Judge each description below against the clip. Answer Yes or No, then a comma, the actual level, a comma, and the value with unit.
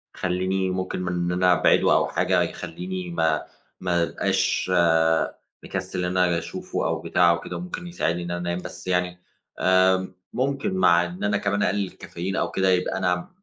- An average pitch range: No, narrow, 1.3 semitones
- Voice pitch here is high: No, very low, 90 Hz